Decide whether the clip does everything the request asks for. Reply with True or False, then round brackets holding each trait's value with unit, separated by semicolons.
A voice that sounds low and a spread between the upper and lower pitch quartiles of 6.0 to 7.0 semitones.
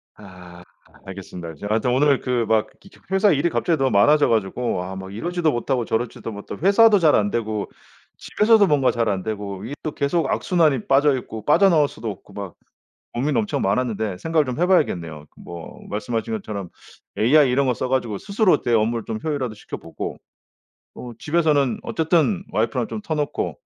True (125 Hz; 6.4 semitones)